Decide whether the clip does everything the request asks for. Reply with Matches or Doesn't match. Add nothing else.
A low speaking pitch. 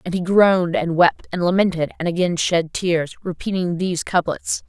Doesn't match